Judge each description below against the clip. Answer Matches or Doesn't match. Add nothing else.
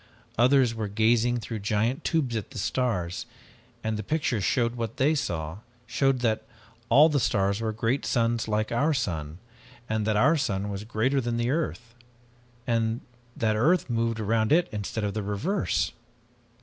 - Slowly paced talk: Doesn't match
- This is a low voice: Matches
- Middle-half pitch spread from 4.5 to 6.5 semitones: Doesn't match